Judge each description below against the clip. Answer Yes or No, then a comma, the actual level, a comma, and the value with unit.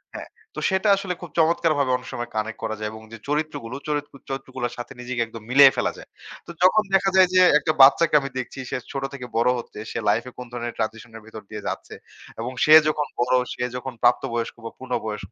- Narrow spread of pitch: No, average, 4.6 semitones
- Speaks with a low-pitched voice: Yes, low, 125 Hz